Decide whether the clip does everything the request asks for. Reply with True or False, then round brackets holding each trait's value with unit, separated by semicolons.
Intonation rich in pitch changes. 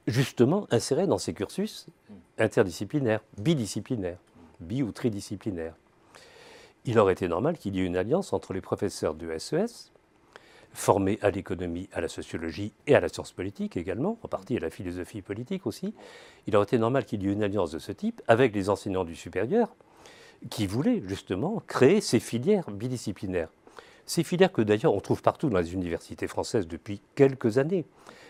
True (6.5 semitones)